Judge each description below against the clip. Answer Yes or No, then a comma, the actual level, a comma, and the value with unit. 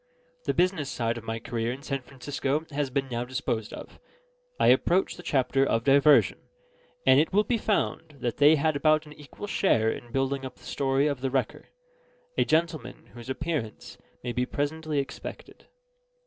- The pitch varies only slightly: No, average, 3.7 semitones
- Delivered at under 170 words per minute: No, average, 175 wpm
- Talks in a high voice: No, medium, 140 Hz